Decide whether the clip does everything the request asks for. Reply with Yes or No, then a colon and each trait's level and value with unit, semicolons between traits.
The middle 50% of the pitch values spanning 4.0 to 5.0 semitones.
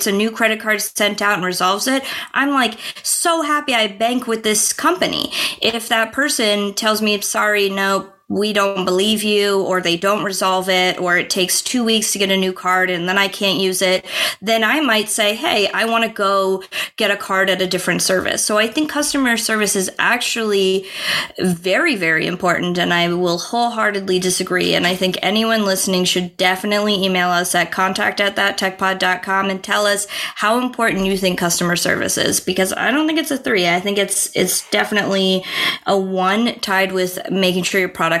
No: average, 3.0 semitones